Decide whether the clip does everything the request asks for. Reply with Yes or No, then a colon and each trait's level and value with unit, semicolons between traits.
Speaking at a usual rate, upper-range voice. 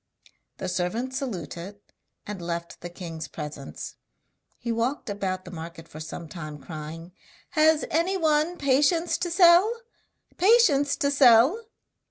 No: slow, 125 wpm; high, 230 Hz